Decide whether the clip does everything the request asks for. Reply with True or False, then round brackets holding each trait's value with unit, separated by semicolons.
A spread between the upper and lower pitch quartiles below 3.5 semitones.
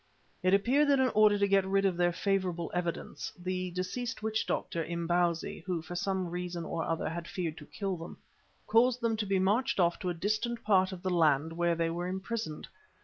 True (3.1 semitones)